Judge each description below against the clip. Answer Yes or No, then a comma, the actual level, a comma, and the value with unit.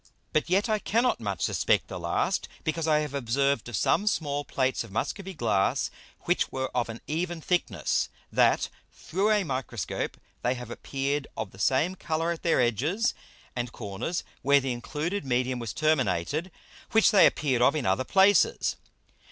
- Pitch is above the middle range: No, medium, 140 Hz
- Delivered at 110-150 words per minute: No, average, 170 wpm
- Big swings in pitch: Yes, wide, 5.9 semitones